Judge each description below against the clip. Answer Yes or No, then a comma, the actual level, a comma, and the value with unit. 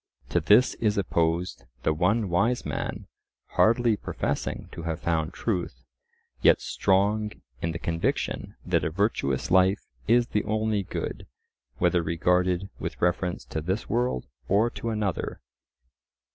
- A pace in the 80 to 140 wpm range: Yes, slow, 135 wpm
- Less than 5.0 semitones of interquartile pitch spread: Yes, average, 4.2 semitones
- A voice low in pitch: Yes, very low, 95 Hz